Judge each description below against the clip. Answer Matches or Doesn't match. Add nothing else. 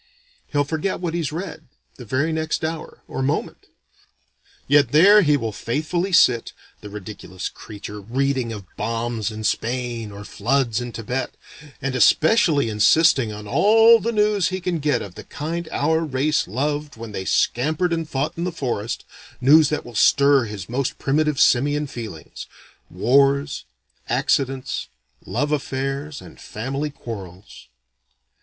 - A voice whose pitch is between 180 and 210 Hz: Doesn't match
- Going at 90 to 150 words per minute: Matches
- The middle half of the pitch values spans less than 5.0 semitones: Doesn't match